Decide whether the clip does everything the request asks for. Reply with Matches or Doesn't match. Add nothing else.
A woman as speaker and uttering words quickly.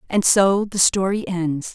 Doesn't match